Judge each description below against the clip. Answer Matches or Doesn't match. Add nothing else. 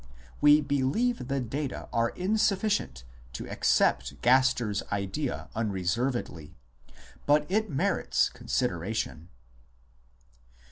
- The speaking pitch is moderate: Doesn't match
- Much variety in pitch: Matches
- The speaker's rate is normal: Doesn't match